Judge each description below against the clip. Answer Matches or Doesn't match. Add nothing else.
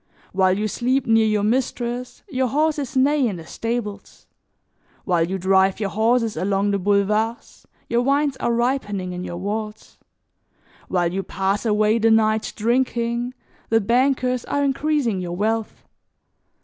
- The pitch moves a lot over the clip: Doesn't match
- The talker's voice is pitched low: Doesn't match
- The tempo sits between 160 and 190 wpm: Doesn't match